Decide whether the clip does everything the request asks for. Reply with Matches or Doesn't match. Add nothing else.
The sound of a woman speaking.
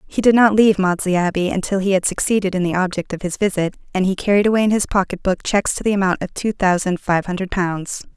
Matches